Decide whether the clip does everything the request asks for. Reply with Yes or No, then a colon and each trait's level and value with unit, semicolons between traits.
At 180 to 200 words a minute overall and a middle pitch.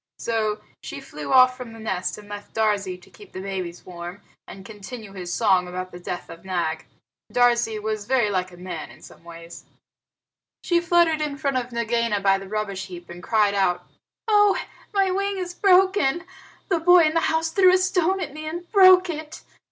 No: average, 195 wpm; high, 225 Hz